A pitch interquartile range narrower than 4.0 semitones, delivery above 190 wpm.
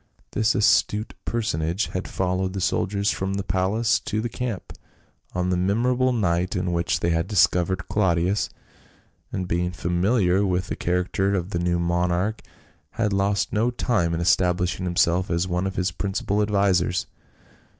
No: narrow, 2.6 semitones; average, 160 wpm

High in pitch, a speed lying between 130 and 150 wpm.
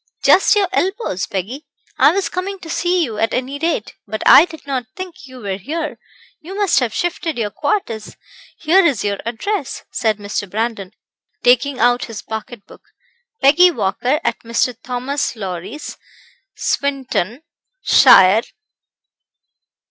Yes: very high, 255 Hz; average, 140 wpm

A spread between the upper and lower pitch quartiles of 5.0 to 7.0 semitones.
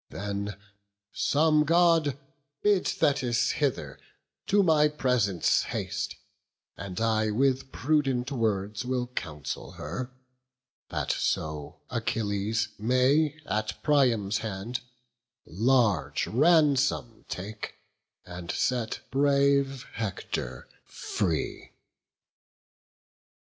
Yes: average, 5.3 semitones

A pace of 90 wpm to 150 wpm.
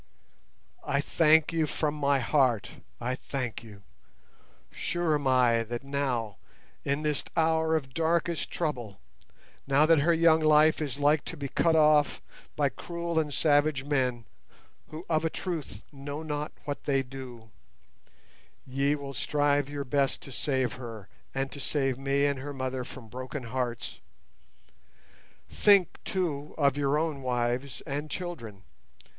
Yes: average, 140 wpm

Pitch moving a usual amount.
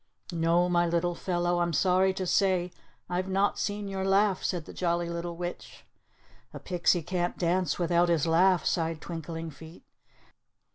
No: narrow, 1.6 semitones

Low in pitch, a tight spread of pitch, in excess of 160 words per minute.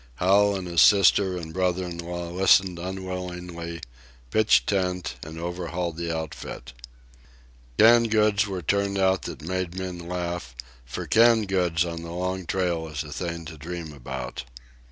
No: very low, 90 Hz; narrow, 2.1 semitones; average, 155 wpm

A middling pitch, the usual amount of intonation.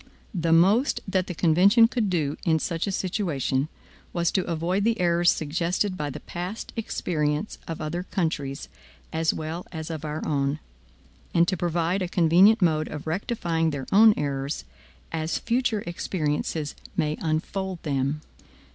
Yes: medium, 170 Hz; average, 3.4 semitones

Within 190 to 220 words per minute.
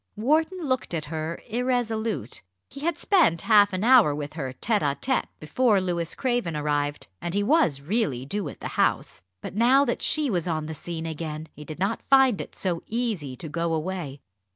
Yes: average, 195 wpm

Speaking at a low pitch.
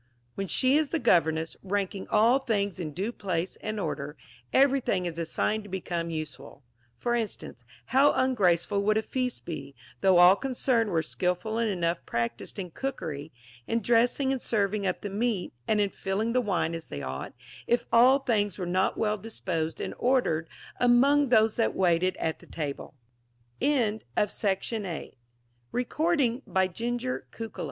No: high, 200 Hz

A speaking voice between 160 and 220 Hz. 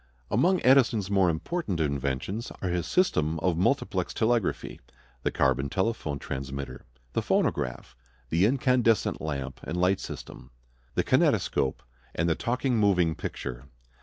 No: very low, 90 Hz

